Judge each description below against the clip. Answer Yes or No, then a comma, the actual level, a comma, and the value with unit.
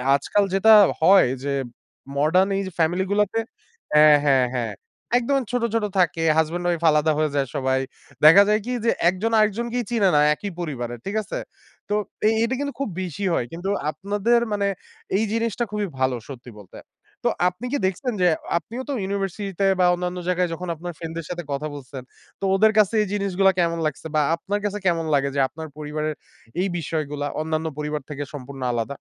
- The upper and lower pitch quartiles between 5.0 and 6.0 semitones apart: Yes, average, 5.3 semitones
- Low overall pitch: No, medium, 175 Hz